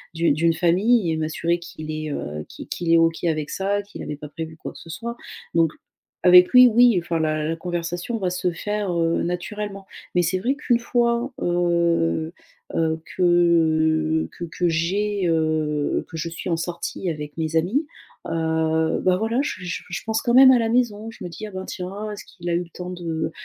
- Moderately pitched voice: Yes, medium, 175 Hz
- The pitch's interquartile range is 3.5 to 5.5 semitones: Yes, average, 4.0 semitones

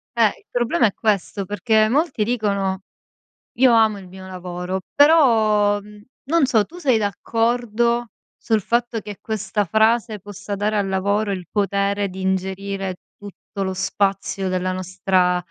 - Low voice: No, high, 205 Hz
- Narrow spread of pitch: No, average, 3.0 semitones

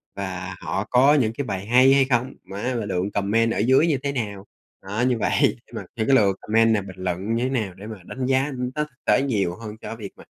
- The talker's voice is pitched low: Yes, low, 115 Hz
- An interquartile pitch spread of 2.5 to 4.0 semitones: No, average, 4.7 semitones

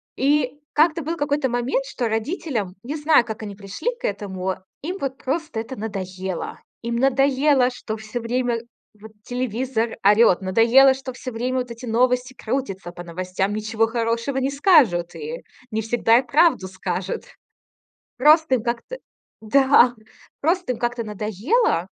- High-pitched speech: Yes, high, 240 Hz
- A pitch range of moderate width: Yes, average, 3.9 semitones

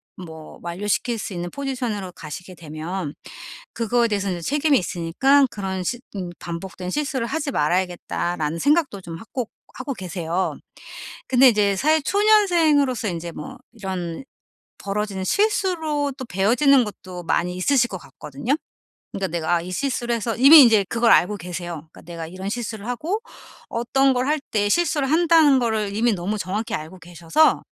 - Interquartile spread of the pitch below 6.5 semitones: No, wide, 7.3 semitones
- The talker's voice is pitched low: No, high, 210 Hz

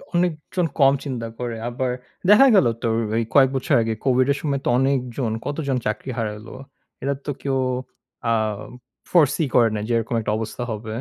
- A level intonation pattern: No, average, 3.6 semitones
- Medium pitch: No, low, 130 Hz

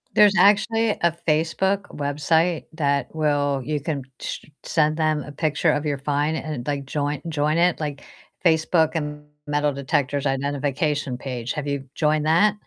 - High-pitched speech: No, medium, 150 Hz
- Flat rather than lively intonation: Yes, narrow, 2.1 semitones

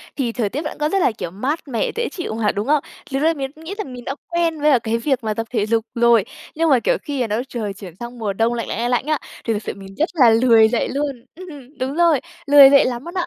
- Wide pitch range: No, average, 4.8 semitones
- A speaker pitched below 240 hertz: No, very high, 255 Hz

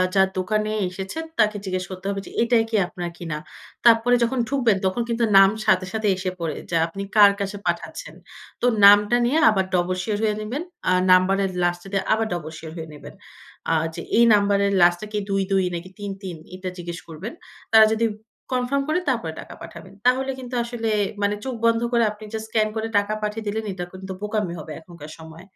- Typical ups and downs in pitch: Yes, average, 3.5 semitones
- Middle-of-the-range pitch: No, high, 200 Hz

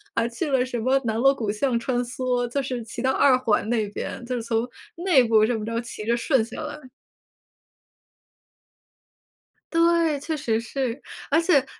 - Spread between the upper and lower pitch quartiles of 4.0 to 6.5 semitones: No, average, 3.1 semitones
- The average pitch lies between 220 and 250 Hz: Yes, high, 245 Hz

